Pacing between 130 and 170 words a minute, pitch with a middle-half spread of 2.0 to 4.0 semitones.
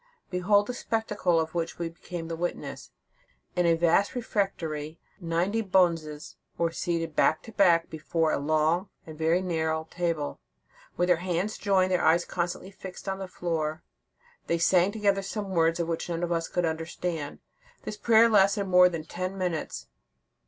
Yes: average, 165 wpm; average, 2.7 semitones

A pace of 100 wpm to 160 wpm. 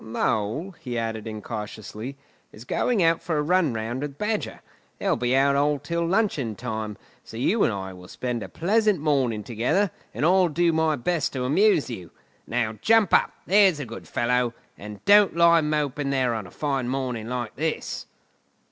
No: average, 175 wpm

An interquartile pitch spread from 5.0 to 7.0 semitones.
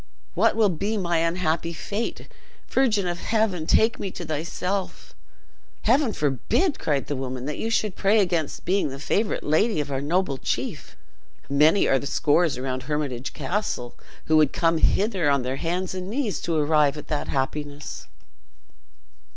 Yes: wide, 5.5 semitones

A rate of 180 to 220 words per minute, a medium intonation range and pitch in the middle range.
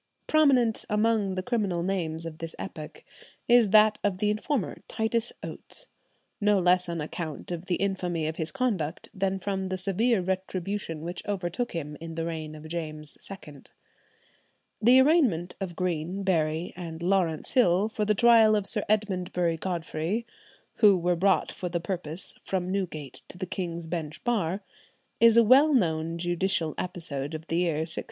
No: average, 165 wpm; average, 4.1 semitones; medium, 180 Hz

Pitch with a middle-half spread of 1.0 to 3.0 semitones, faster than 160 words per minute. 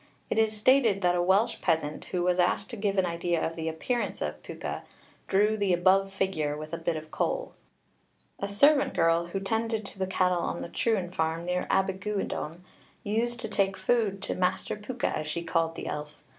No: average, 3.7 semitones; average, 200 wpm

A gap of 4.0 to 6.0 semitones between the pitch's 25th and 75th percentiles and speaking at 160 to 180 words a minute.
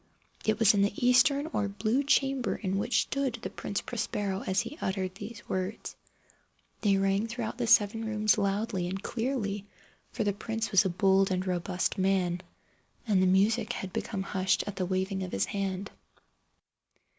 No: average, 2.8 semitones; average, 170 wpm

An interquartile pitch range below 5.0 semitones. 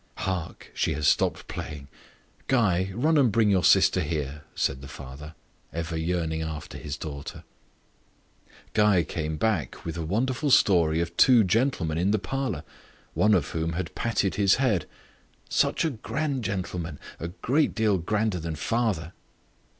No: wide, 5.6 semitones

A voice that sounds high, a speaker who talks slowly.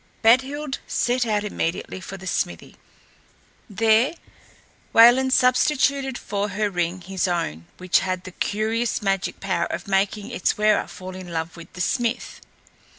No: high, 205 Hz; average, 145 wpm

